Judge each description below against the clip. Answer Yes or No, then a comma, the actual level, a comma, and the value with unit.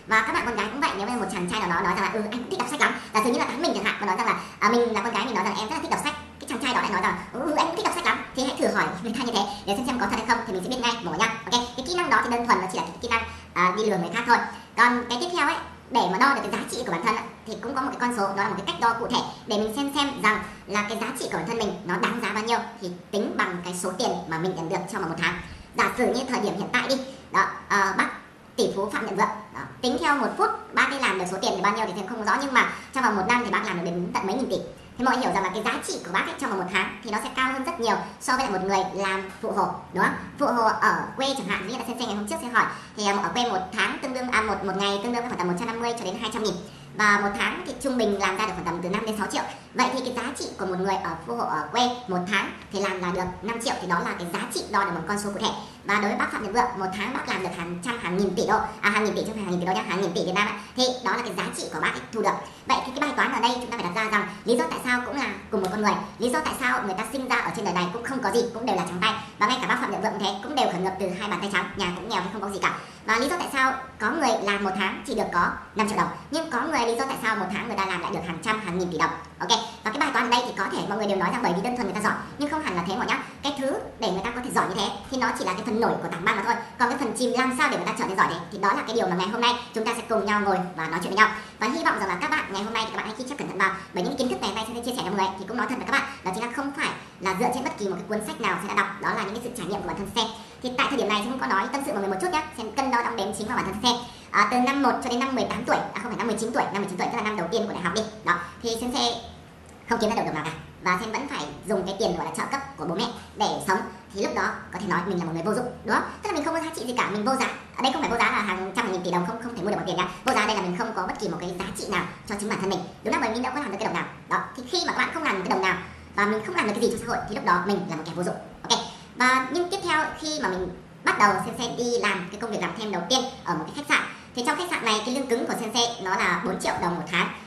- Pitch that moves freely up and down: No, average, 4.0 semitones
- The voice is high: Yes, high, 215 Hz